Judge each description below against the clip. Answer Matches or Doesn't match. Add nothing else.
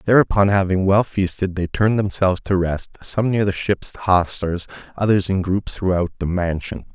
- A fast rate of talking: Doesn't match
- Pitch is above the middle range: Doesn't match